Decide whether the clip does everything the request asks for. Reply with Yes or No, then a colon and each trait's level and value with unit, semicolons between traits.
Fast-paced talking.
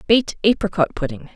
No: slow, 135 wpm